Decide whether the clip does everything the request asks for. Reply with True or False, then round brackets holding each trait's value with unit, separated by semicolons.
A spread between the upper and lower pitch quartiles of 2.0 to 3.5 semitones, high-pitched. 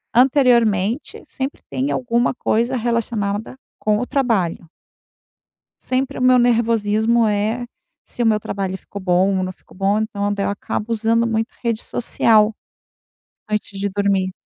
True (2.9 semitones; 220 Hz)